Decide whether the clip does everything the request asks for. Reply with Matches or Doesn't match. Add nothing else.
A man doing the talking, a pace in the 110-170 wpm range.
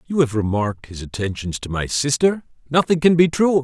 Doesn't match